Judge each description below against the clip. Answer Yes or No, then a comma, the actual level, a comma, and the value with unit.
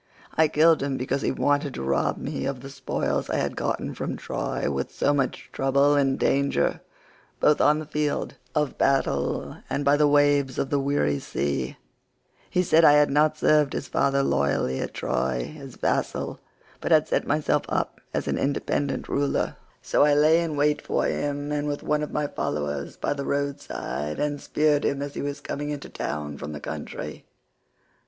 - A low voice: No, medium, 145 Hz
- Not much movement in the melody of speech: Yes, narrow, 1.7 semitones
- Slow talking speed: No, average, 185 wpm